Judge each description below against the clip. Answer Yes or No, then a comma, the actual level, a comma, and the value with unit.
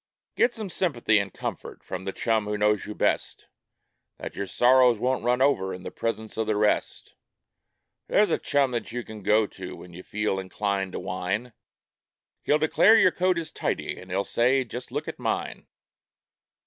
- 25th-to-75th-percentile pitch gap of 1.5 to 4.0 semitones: No, average, 4.7 semitones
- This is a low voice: Yes, low, 110 Hz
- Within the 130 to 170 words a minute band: No, average, 185 wpm